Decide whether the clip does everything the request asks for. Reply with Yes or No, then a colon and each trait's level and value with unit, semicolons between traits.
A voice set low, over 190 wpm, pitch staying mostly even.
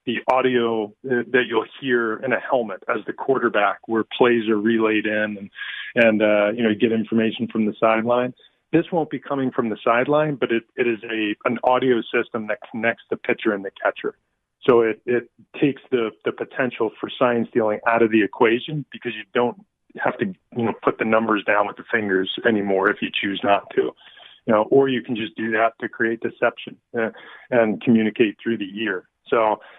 Yes: low, 115 Hz; average, 200 wpm; narrow, 2.1 semitones